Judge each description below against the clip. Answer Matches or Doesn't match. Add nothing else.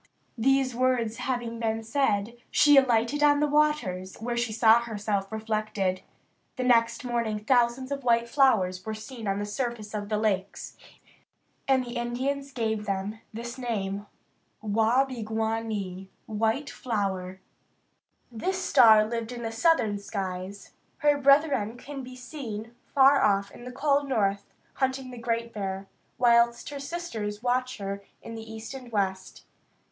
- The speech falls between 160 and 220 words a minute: Doesn't match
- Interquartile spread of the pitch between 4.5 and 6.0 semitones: Doesn't match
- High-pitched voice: Matches